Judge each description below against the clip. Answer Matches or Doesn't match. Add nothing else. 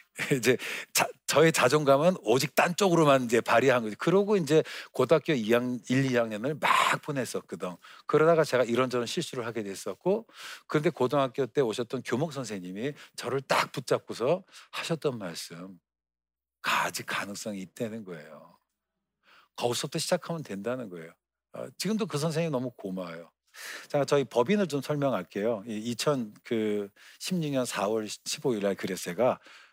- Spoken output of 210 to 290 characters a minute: Doesn't match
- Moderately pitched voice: Doesn't match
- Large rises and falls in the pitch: Matches